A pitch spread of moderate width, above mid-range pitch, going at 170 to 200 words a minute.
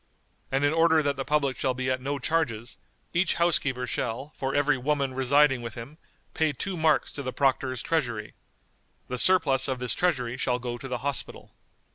No: average, 3.0 semitones; low, 135 Hz; average, 185 wpm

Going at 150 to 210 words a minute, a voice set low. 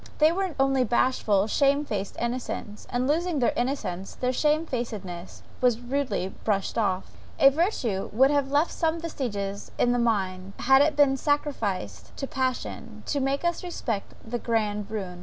No: average, 165 wpm; high, 245 Hz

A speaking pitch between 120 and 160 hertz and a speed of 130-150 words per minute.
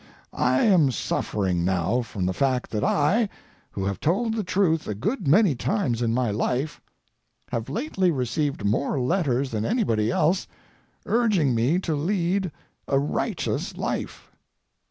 Yes: medium, 140 Hz; average, 145 wpm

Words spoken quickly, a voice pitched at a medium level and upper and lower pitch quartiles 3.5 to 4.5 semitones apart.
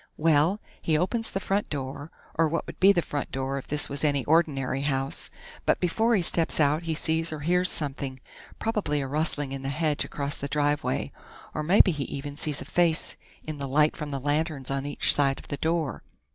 No: fast, 210 wpm; medium, 150 Hz; average, 2.8 semitones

